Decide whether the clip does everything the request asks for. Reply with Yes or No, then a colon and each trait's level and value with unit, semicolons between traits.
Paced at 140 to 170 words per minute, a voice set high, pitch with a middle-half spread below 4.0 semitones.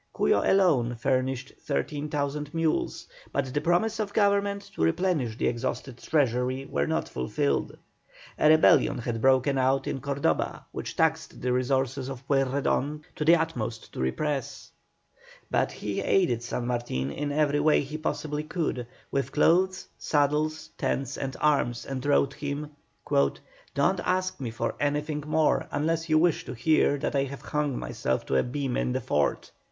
No: average, 160 wpm; medium, 140 Hz; average, 3.6 semitones